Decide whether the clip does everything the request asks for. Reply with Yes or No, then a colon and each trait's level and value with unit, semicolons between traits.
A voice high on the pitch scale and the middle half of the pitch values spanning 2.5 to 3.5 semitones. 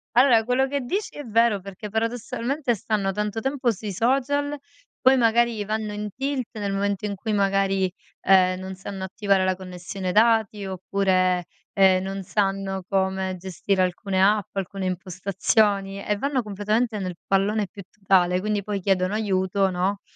Yes: high, 200 Hz; average, 2.8 semitones